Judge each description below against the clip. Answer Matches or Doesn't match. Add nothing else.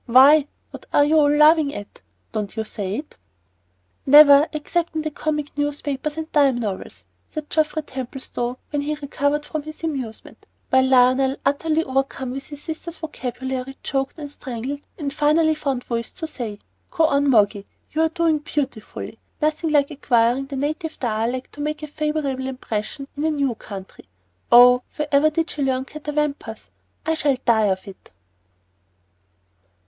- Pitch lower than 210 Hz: Doesn't match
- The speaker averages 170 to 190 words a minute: Doesn't match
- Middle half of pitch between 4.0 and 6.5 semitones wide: Doesn't match